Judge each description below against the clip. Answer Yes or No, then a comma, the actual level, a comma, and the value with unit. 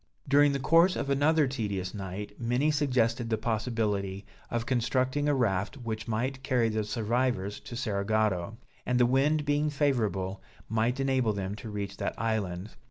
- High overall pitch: No, low, 115 Hz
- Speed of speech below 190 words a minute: Yes, average, 160 wpm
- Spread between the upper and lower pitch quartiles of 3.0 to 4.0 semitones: No, average, 4.4 semitones